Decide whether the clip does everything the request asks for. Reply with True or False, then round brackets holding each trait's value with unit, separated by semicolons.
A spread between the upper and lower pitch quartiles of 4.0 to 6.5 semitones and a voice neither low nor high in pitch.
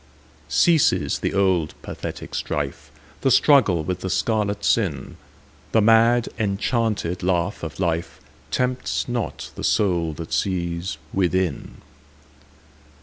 False (4.8 semitones; 95 Hz)